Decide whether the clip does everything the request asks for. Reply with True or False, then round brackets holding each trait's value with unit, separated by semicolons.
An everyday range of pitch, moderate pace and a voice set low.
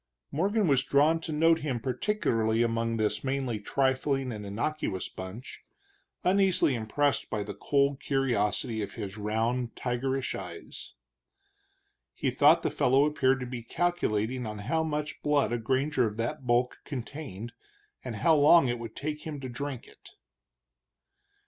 True (4.4 semitones; 150 wpm; 130 Hz)